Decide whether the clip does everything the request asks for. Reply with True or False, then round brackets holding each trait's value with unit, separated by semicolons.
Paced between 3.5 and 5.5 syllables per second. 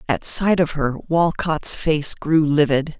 True (3.7 syllables/s)